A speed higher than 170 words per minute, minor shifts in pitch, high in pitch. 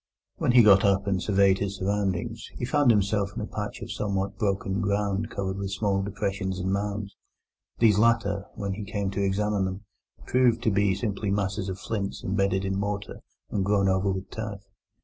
No: average, 190 wpm; narrow, 1.3 semitones; low, 100 Hz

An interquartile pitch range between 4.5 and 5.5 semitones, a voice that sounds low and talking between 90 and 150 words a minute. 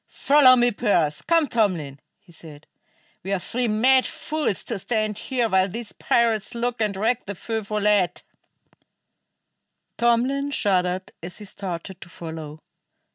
No: average, 4.8 semitones; high, 210 Hz; average, 140 wpm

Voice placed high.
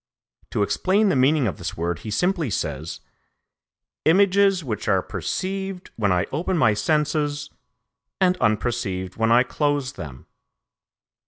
No: low, 135 Hz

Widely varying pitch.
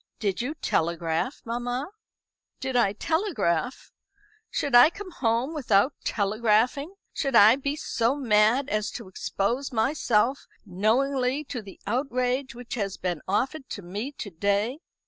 No: average, 4.8 semitones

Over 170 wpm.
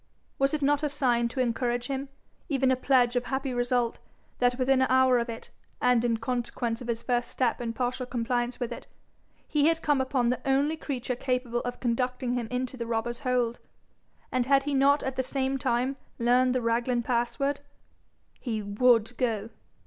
Yes: average, 185 wpm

